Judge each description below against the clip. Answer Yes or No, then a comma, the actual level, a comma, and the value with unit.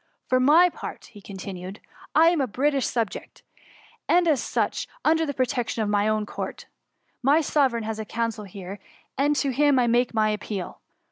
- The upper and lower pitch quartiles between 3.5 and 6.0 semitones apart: Yes, average, 5.2 semitones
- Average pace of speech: Yes, average, 190 wpm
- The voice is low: No, high, 240 Hz